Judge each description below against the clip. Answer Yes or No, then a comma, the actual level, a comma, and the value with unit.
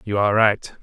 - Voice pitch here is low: Yes, low, 105 Hz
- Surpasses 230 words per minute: No, fast, 220 wpm